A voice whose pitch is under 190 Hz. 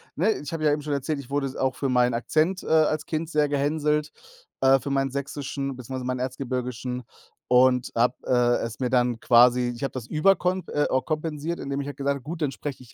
Yes: medium, 140 Hz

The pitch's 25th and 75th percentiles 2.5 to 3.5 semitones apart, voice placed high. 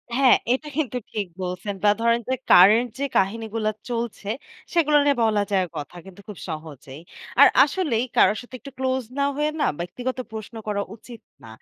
No: average, 4.7 semitones; high, 225 Hz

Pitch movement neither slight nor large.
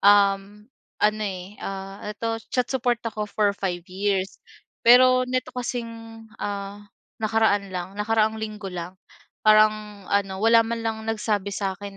No: narrow, 2.3 semitones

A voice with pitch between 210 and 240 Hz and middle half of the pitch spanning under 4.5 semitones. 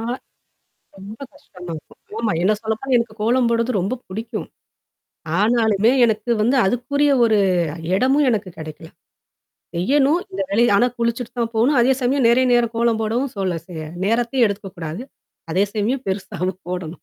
Yes: high, 225 Hz; average, 3.9 semitones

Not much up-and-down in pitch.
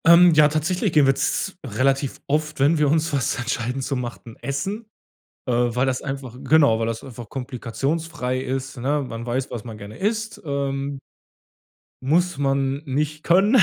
No: average, 3.7 semitones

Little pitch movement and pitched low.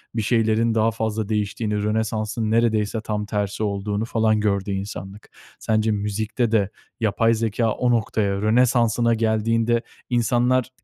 Yes: narrow, 1.6 semitones; low, 110 Hz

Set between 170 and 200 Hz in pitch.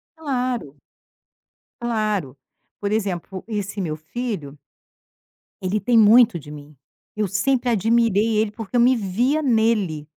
No: high, 215 Hz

